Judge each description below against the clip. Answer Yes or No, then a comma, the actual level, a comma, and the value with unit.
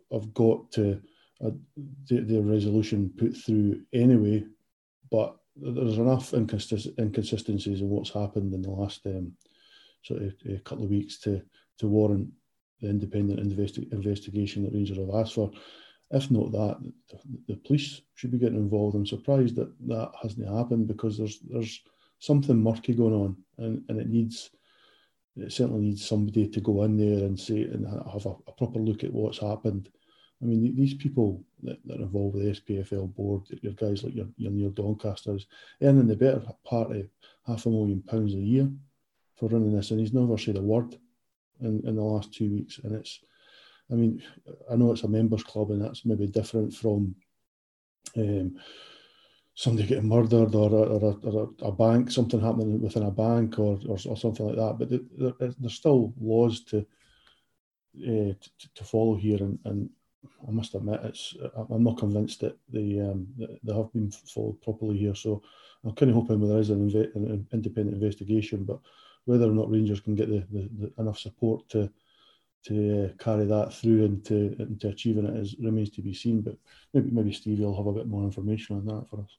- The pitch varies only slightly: Yes, narrow, 1.8 semitones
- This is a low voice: Yes, low, 110 Hz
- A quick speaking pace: No, average, 190 wpm